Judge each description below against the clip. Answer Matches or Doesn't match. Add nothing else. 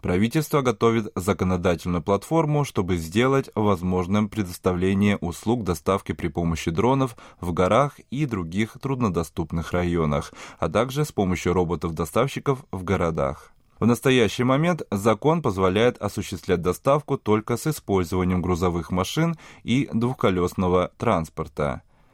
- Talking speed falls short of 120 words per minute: Matches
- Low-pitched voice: Matches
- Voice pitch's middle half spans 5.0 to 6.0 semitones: Matches